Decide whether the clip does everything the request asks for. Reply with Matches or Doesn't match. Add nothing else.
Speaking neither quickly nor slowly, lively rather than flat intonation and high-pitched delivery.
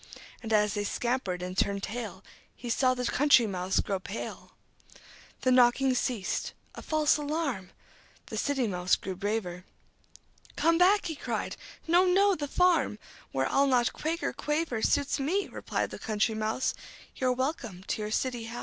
Matches